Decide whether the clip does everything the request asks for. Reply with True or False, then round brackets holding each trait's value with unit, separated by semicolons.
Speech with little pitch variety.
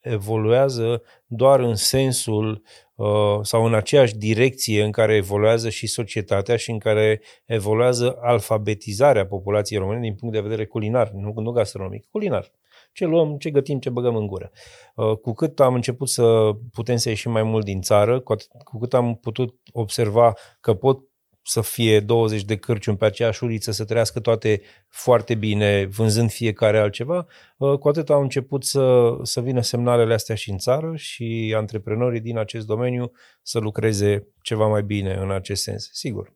True (2.3 semitones)